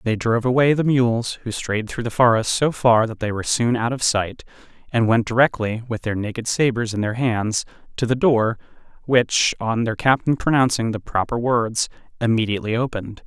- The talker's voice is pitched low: Yes, low, 115 Hz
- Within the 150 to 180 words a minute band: No, average, 190 wpm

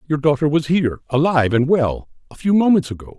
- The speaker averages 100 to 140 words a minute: No, fast, 205 wpm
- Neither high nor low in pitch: Yes, medium, 150 Hz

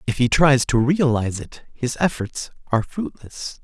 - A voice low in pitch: Yes, low, 130 Hz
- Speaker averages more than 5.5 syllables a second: No, 4.6 syllables/s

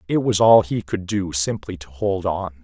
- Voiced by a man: Yes, male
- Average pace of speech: No, fast, 230 wpm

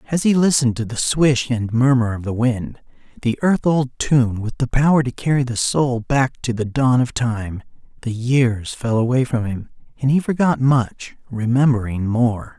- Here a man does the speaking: Yes, male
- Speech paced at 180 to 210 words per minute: Yes, average, 190 wpm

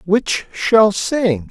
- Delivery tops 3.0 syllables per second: No, 2.3 syllables/s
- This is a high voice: Yes, high, 200 Hz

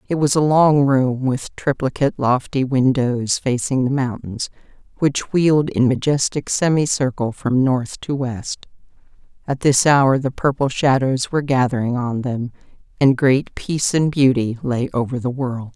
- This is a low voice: Yes, low, 130 Hz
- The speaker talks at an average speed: Yes, average, 150 wpm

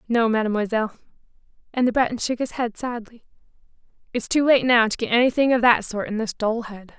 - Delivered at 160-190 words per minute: No, average, 200 wpm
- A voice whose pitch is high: Yes, high, 235 Hz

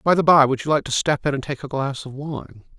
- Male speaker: Yes, male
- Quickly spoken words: Yes, fast, 325 wpm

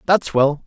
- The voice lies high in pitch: No, medium, 155 Hz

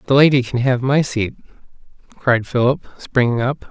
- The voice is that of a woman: No, male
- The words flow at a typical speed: Yes, average, 160 wpm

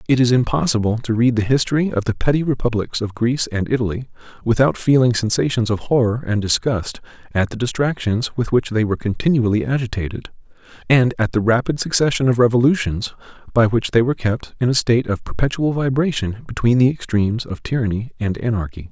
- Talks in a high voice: No, low, 120 Hz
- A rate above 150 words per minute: Yes, average, 180 wpm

